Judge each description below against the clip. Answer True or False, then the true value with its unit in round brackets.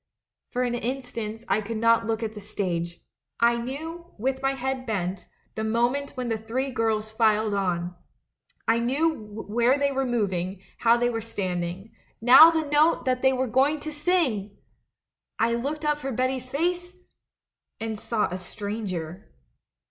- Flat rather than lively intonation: False (4.0 semitones)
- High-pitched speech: True (235 Hz)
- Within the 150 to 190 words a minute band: True (165 wpm)